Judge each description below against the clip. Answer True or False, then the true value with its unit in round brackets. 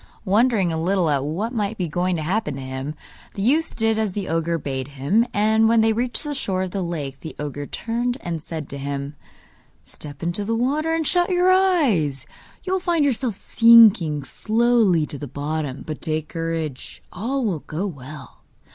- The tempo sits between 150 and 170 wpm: False (190 wpm)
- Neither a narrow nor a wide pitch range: False (7.4 semitones)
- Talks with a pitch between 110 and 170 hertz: False (185 Hz)